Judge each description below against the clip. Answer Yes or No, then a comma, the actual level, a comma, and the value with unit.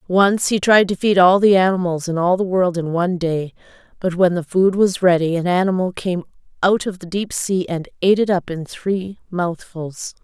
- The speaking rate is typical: No, fast, 210 wpm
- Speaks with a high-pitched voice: No, medium, 180 Hz